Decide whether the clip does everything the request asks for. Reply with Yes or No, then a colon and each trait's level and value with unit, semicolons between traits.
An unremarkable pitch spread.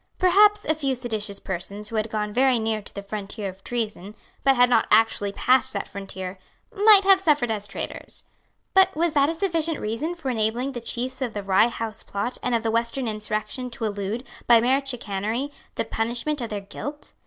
Yes: average, 4.5 semitones